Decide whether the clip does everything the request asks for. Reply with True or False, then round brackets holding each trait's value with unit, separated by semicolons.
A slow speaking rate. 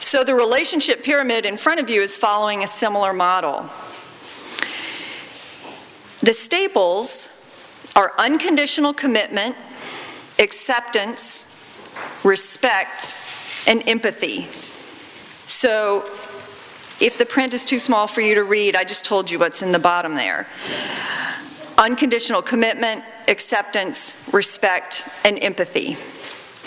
True (110 wpm)